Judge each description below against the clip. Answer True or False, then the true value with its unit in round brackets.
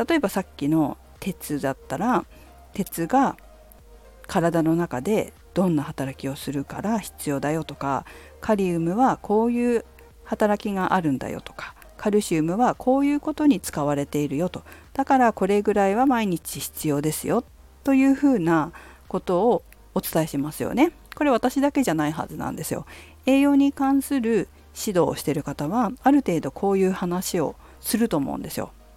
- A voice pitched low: False (190 Hz)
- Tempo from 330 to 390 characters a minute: True (350 characters per minute)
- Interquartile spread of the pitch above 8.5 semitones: True (8.9 semitones)